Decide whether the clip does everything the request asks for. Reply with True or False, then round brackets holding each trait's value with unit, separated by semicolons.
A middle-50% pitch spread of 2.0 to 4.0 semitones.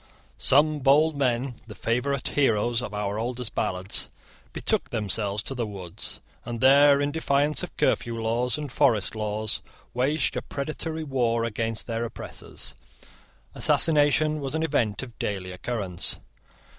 False (4.7 semitones)